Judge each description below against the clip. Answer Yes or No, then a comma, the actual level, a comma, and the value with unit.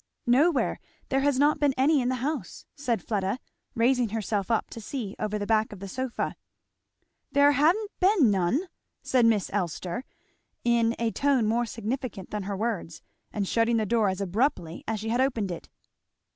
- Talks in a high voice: Yes, high, 230 Hz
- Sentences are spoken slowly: No, average, 175 wpm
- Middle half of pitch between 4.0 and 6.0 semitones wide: Yes, average, 4.3 semitones